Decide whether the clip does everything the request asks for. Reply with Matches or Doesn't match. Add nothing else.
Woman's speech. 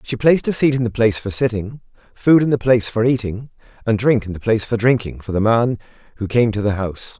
Doesn't match